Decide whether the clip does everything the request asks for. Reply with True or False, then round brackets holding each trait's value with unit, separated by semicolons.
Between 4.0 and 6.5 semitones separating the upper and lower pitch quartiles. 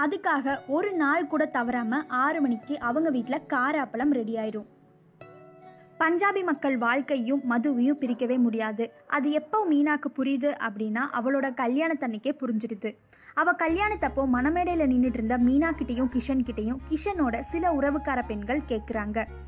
False (3.6 semitones)